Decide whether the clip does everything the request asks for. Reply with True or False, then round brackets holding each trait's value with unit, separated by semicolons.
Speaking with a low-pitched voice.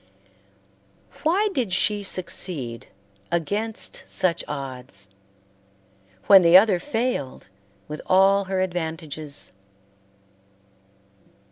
False (185 Hz)